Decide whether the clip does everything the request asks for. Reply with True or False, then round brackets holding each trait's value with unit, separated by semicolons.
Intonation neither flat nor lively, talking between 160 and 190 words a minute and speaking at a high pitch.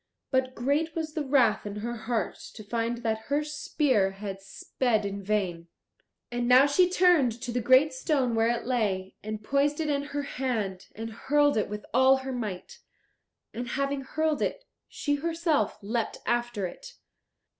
True (4.9 semitones; 170 wpm; 245 Hz)